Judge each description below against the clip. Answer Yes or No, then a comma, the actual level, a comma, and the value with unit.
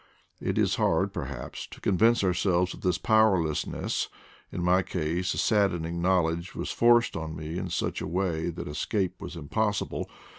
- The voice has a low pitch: Yes, very low, 90 Hz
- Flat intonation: No, average, 3.0 semitones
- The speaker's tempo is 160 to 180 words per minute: Yes, average, 170 wpm